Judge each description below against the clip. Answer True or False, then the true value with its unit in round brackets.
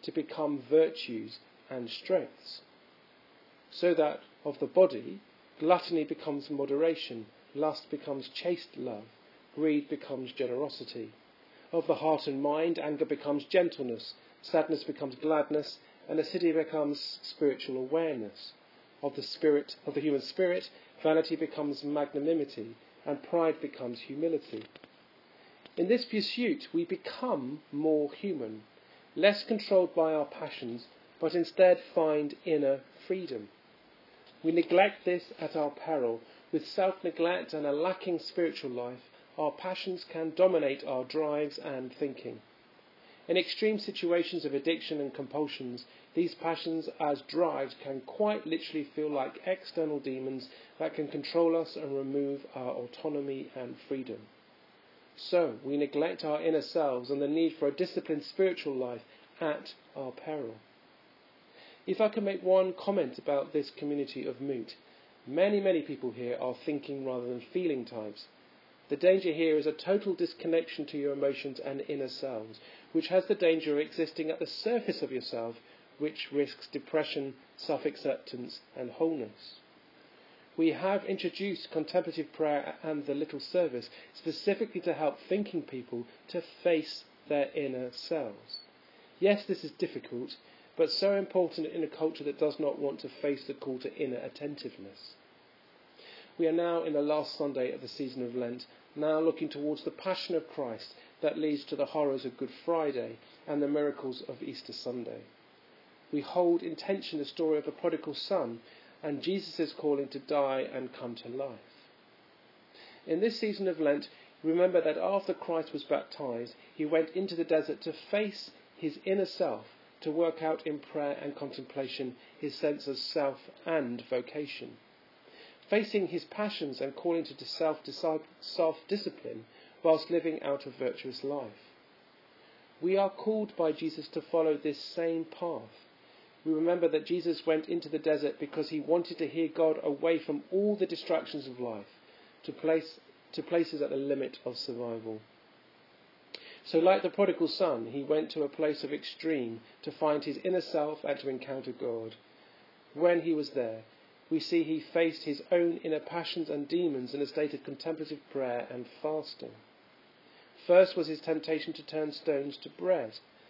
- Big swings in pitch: False (3.2 semitones)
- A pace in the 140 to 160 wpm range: True (155 wpm)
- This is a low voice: False (155 Hz)